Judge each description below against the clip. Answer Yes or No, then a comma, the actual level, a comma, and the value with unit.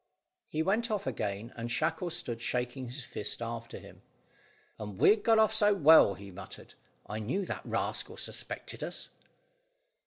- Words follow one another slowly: No, average, 155 wpm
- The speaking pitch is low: Yes, low, 125 Hz